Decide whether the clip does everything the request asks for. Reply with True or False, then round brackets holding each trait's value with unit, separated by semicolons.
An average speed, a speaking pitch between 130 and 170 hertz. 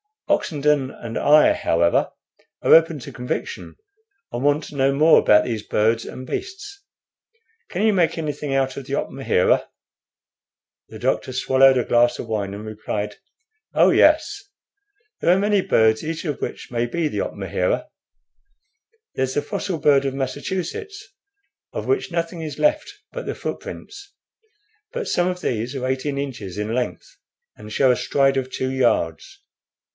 True (155 wpm; 140 Hz)